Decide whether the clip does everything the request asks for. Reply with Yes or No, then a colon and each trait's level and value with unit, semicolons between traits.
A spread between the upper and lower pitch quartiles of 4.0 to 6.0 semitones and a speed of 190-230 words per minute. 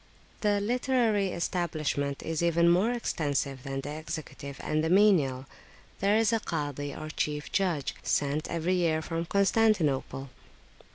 No: wide, 5.5 semitones; slow, 135 wpm